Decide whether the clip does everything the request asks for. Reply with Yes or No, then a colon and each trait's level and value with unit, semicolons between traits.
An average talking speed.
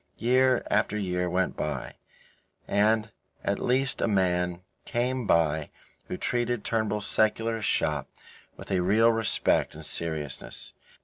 No: slow, 130 wpm